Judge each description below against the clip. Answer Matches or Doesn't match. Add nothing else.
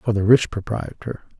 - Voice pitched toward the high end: Doesn't match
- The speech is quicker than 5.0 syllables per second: Doesn't match